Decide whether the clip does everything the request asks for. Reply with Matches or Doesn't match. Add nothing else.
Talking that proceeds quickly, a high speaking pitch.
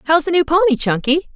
Matches